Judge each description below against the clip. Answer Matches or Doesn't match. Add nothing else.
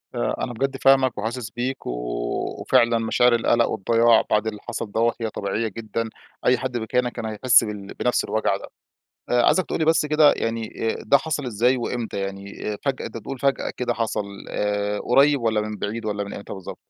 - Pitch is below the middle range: Matches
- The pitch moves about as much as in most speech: Matches